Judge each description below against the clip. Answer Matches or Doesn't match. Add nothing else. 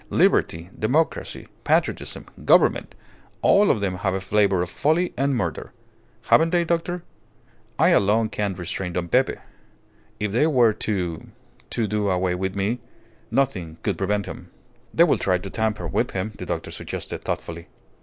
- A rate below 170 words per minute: Matches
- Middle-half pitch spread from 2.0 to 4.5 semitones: Doesn't match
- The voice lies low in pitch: Matches